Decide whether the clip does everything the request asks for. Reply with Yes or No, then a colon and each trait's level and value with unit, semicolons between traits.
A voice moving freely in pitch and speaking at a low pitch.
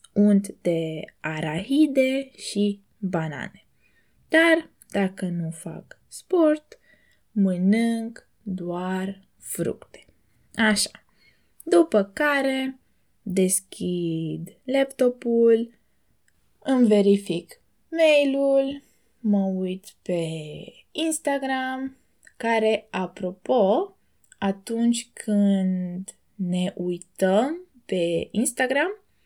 No: wide, 6.2 semitones; high, 205 Hz